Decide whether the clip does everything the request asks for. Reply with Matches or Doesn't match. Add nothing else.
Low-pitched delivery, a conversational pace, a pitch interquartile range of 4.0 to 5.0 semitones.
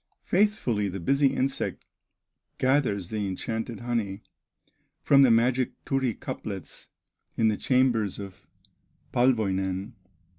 Doesn't match